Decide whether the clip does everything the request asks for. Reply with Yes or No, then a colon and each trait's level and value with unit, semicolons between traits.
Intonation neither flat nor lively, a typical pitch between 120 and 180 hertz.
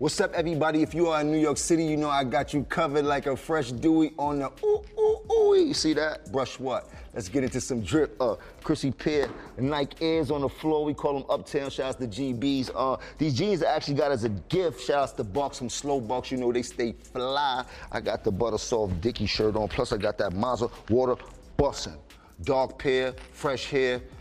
Yes: average, 3.7 semitones; medium, 140 Hz